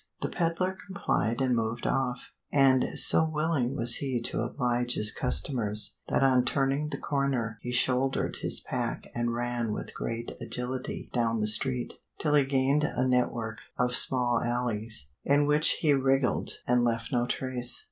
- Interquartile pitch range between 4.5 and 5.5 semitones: No, narrow, 2.5 semitones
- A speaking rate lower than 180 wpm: Yes, average, 160 wpm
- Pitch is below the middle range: Yes, low, 125 Hz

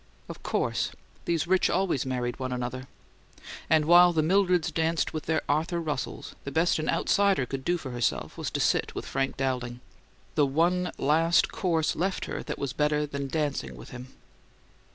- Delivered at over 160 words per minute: Yes, average, 175 wpm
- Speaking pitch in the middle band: Yes, medium, 150 Hz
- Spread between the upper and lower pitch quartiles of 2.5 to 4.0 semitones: No, average, 4.4 semitones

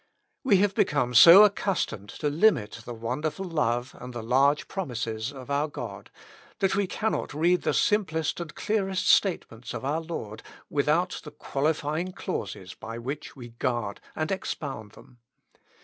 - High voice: No, medium, 150 Hz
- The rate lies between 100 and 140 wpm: No, average, 155 wpm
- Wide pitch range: Yes, wide, 6.7 semitones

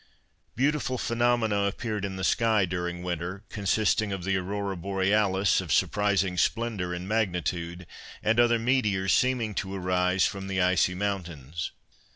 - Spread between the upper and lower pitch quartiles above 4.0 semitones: No, average, 3.2 semitones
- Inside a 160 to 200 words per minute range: No, average, 140 wpm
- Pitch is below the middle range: Yes, very low, 95 Hz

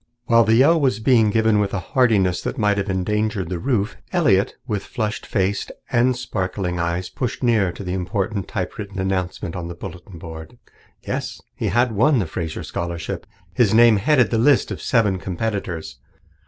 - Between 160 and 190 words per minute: Yes, average, 175 wpm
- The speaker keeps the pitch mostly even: No, average, 4.1 semitones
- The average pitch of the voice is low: Yes, low, 105 Hz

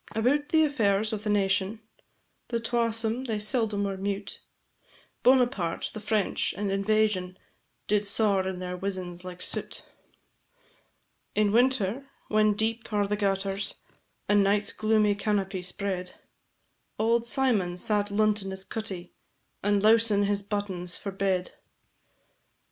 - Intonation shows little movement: Yes, narrow, 2.2 semitones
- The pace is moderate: No, slow, 125 wpm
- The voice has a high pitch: Yes, high, 205 Hz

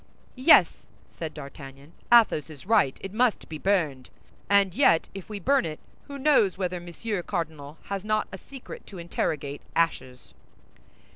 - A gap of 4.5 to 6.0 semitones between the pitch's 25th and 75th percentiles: Yes, average, 5.2 semitones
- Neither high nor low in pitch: Yes, medium, 175 Hz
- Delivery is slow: No, average, 150 wpm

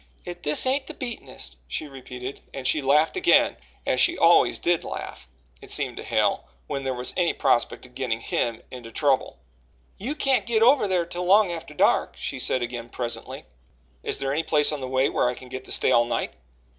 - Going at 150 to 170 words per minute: No, fast, 205 wpm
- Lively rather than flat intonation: Yes, wide, 5.9 semitones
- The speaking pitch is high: No, medium, 140 Hz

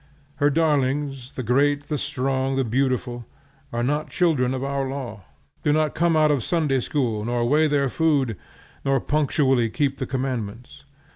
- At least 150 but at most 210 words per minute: Yes, average, 165 wpm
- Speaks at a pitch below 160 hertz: Yes, low, 135 Hz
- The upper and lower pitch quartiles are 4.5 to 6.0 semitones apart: No, average, 2.7 semitones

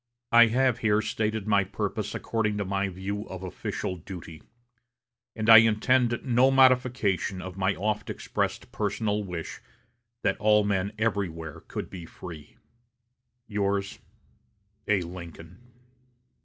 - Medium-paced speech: No, slow, 125 wpm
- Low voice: Yes, low, 100 Hz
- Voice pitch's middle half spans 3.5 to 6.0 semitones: No, average, 3.0 semitones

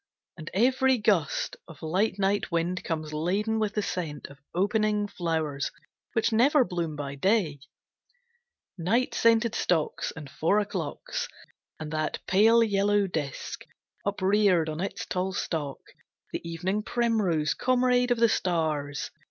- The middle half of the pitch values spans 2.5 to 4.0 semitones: No, wide, 5.6 semitones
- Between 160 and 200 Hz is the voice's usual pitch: Yes, high, 190 Hz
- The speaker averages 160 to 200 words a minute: No, slow, 135 wpm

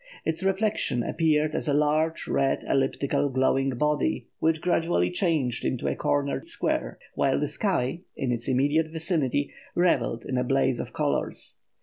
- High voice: No, medium, 150 Hz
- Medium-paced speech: Yes, average, 150 wpm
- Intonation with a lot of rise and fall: No, average, 3.5 semitones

